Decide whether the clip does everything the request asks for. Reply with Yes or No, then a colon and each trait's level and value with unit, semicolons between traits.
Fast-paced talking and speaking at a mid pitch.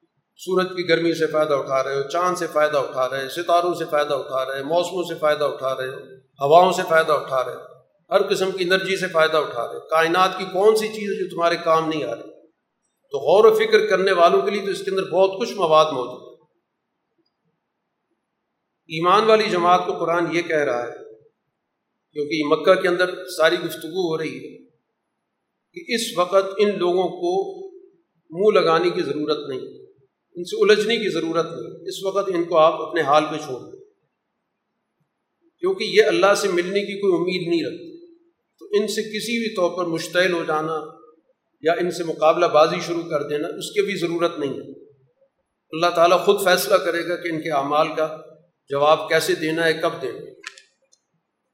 Yes: fast, 195 wpm; medium, 175 Hz